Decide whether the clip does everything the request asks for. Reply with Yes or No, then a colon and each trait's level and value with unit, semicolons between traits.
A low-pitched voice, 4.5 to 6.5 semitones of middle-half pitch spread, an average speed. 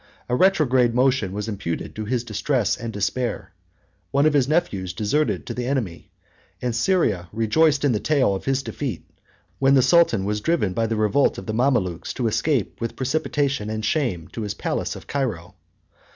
Yes: low, 120 Hz; average, 5.0 semitones; average, 180 wpm